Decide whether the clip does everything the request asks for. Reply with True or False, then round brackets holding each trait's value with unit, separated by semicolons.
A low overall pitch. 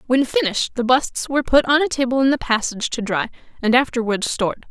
False (250 Hz)